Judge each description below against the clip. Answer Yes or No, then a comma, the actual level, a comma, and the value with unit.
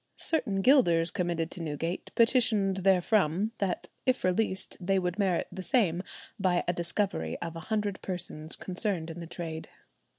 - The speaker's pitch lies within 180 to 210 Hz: Yes, medium, 185 Hz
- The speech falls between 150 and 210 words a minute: Yes, average, 155 wpm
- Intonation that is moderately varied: Yes, average, 3.3 semitones